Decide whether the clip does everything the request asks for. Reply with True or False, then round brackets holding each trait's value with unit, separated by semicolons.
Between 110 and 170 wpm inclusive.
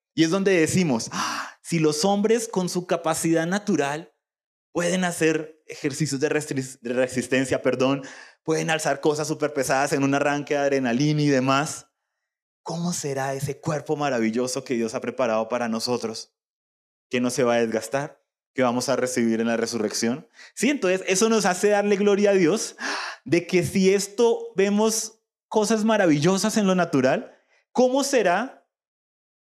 True (155 wpm)